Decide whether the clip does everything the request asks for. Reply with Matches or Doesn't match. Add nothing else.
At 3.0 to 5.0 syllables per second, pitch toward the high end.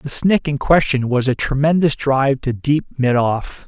Doesn't match